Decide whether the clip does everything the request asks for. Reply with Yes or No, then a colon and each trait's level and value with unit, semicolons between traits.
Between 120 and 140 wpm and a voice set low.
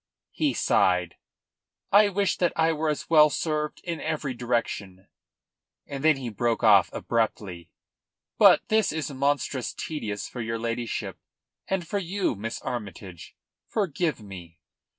Yes: slow, 135 wpm; low, 125 Hz